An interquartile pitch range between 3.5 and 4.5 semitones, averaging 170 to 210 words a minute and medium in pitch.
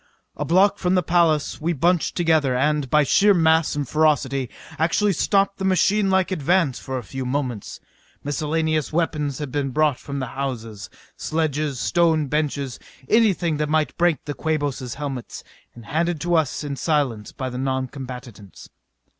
No: average, 3.9 semitones; average, 155 wpm; medium, 150 Hz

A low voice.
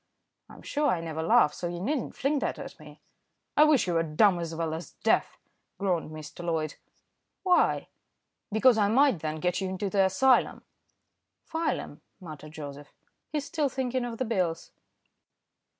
No: medium, 185 Hz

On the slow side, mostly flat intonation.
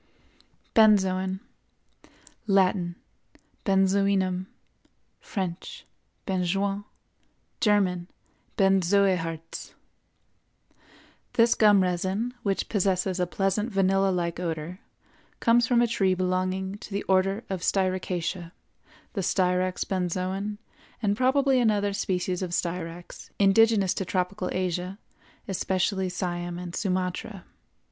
Yes: slow, 90 wpm; narrow, 1.8 semitones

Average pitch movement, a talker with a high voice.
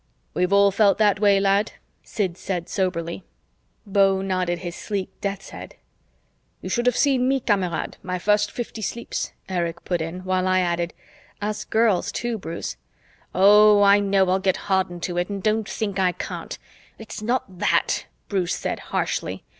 No: narrow, 2.3 semitones; high, 195 Hz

